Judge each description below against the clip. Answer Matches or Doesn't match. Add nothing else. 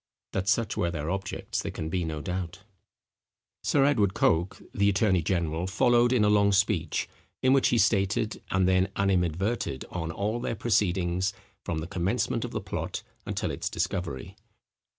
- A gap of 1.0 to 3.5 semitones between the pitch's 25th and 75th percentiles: Matches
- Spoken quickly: Doesn't match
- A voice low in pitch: Matches